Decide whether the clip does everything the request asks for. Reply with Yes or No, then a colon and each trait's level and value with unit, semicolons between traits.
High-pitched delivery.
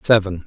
No: low, 100 Hz